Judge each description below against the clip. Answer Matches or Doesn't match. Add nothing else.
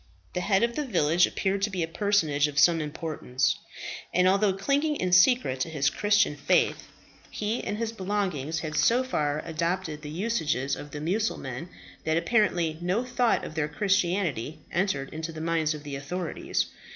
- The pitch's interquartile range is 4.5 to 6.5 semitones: Matches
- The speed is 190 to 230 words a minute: Doesn't match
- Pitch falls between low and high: Matches